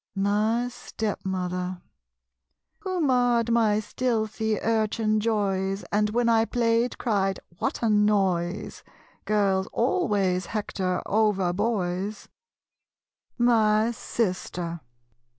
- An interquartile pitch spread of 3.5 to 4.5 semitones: No, average, 3.1 semitones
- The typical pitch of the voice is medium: No, high, 210 Hz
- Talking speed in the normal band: No, slow, 90 wpm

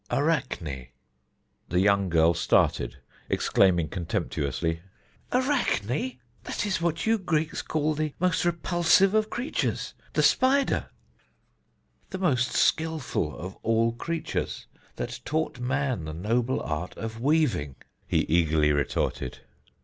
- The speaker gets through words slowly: Yes, slow, 120 wpm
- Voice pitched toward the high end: No, low, 125 Hz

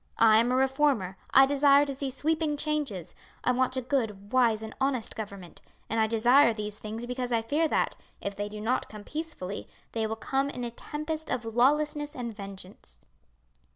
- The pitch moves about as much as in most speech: Yes, average, 4.5 semitones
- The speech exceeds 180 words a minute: Yes, average, 190 wpm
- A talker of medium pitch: No, high, 245 Hz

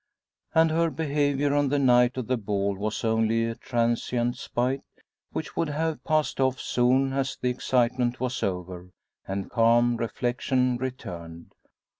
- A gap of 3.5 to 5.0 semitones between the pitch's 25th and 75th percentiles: No, average, 2.9 semitones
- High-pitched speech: No, low, 125 Hz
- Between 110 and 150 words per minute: Yes, average, 145 wpm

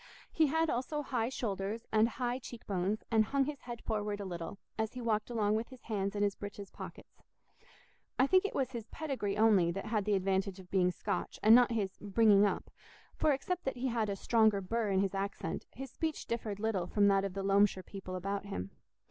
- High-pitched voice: Yes, high, 210 Hz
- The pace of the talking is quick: Yes, fast, 215 wpm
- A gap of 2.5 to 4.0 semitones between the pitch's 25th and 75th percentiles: Yes, average, 3.4 semitones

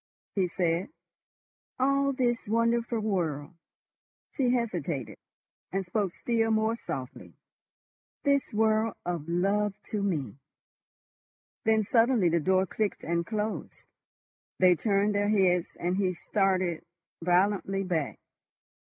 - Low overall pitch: No, high, 195 Hz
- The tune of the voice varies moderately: Yes, average, 4.0 semitones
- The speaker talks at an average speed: No, slow, 110 wpm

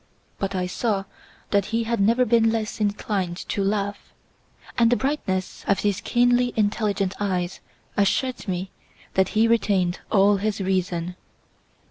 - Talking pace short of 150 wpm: Yes, average, 140 wpm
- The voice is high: Yes, high, 205 Hz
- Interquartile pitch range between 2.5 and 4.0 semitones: Yes, average, 3.0 semitones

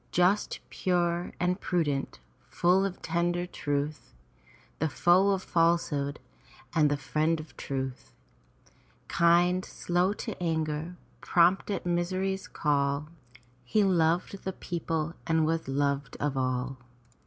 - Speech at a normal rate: No, slow, 120 wpm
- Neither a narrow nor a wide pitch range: Yes, average, 3.4 semitones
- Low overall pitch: No, medium, 170 Hz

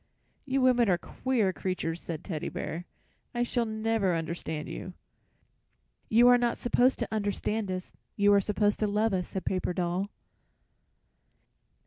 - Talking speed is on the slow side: No, average, 145 wpm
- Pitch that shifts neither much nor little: Yes, average, 4.2 semitones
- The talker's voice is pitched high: Yes, high, 205 Hz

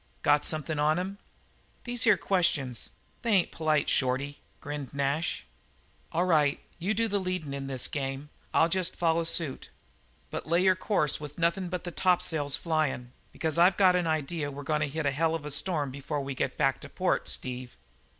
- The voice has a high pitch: No, medium, 155 Hz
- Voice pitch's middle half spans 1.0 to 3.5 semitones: No, average, 3.9 semitones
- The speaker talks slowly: No, average, 190 wpm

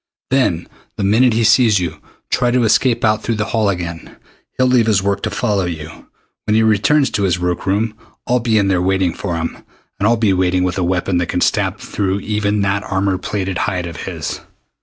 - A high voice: No, low, 100 Hz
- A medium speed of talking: No, fast, 215 wpm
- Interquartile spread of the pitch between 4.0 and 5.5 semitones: No, average, 3.4 semitones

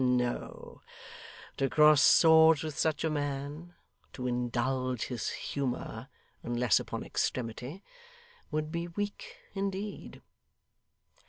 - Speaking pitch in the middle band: Yes, medium, 145 Hz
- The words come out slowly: Yes, slow, 100 wpm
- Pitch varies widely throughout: No, average, 4.3 semitones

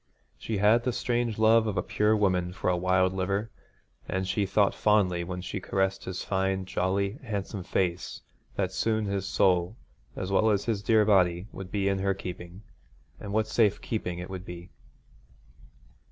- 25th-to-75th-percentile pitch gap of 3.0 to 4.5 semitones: No, narrow, 2.5 semitones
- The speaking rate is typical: Yes, average, 175 wpm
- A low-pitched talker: Yes, very low, 95 Hz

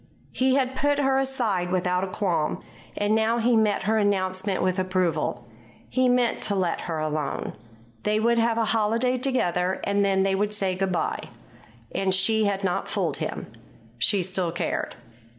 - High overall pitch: Yes, high, 200 Hz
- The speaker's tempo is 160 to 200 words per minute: Yes, average, 170 wpm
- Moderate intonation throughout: Yes, average, 3.7 semitones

